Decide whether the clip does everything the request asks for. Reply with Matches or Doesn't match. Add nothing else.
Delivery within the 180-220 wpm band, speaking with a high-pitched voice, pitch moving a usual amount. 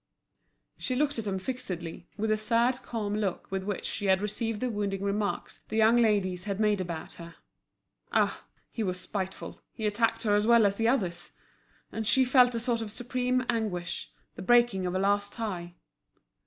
Matches